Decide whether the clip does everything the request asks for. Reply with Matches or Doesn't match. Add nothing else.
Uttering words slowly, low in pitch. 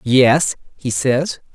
Matches